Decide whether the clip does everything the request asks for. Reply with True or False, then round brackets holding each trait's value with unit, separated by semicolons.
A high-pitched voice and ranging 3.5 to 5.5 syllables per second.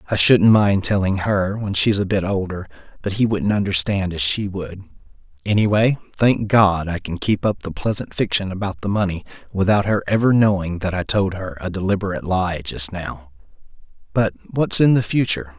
False (100 Hz; 5.1 syllables/s)